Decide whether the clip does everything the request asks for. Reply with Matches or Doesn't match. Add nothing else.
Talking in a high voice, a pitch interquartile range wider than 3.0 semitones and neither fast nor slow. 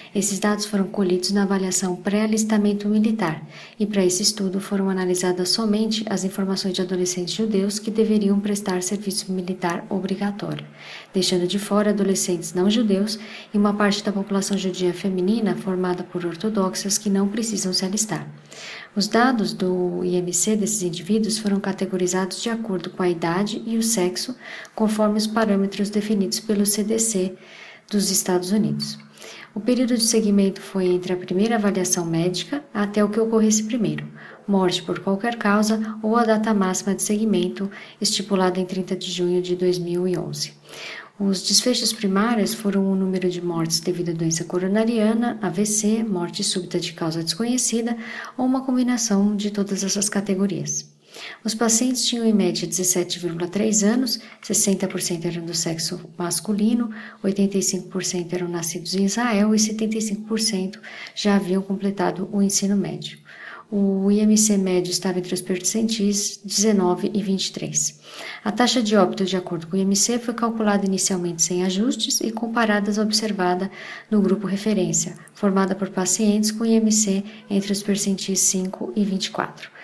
Doesn't match